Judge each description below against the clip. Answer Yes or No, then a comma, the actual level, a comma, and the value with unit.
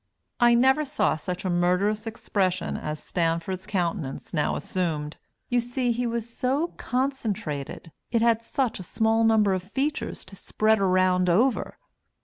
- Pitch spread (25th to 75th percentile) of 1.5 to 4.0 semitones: No, average, 4.9 semitones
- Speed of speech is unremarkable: Yes, average, 145 wpm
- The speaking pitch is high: Yes, high, 210 Hz